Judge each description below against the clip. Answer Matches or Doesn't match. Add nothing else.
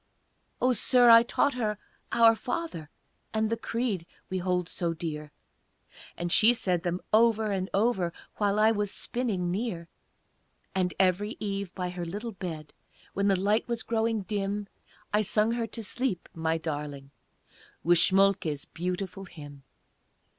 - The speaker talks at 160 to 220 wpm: Doesn't match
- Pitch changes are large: Doesn't match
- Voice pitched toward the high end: Matches